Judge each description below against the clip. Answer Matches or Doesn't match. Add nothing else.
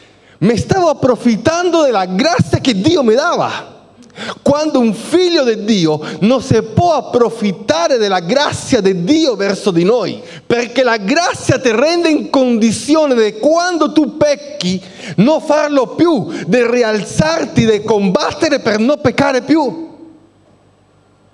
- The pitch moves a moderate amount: Doesn't match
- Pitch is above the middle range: Matches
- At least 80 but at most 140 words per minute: Matches